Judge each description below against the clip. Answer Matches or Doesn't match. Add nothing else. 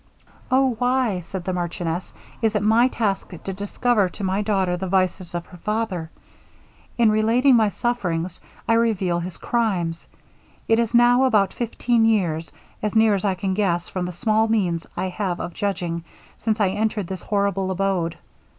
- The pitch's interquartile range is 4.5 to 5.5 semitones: Doesn't match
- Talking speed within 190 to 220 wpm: Doesn't match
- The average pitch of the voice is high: Matches